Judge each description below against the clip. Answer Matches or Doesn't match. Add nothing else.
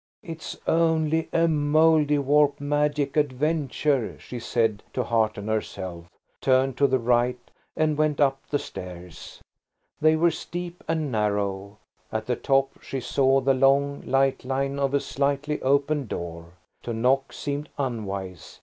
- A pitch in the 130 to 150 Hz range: Matches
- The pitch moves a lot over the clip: Doesn't match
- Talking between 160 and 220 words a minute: Doesn't match